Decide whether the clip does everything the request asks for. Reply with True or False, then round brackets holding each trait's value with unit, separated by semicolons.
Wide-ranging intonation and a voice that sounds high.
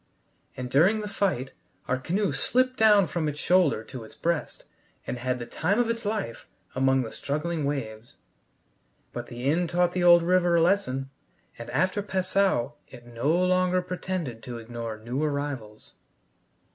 False (6.5 semitones; 155 Hz)